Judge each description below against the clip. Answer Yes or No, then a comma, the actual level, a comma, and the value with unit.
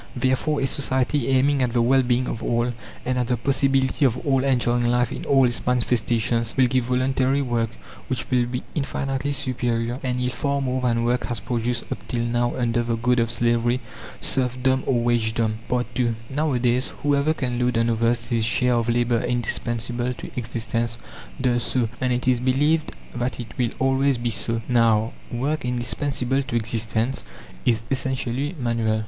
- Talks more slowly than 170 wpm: No, average, 175 wpm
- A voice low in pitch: Yes, low, 125 Hz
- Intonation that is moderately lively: No, narrow, 1.8 semitones